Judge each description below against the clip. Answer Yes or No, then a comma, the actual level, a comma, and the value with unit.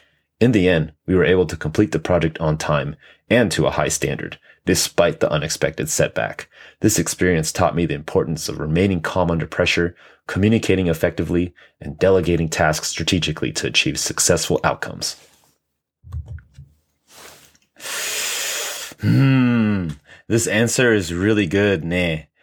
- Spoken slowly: Yes, slow, 130 wpm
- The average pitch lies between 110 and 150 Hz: No, very low, 90 Hz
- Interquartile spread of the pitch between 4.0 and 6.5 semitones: Yes, average, 4.3 semitones